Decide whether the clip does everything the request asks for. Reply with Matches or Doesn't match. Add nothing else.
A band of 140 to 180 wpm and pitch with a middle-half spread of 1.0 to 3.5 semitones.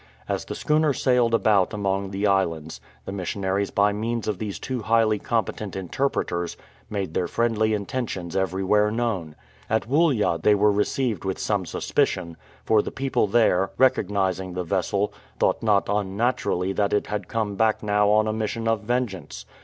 Matches